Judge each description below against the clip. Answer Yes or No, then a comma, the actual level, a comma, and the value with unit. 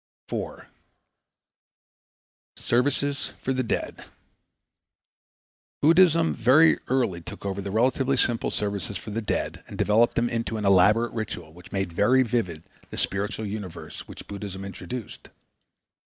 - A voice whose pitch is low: Yes, low, 110 Hz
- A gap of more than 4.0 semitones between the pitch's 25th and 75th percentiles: Yes, average, 4.4 semitones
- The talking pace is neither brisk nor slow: No, slow, 125 wpm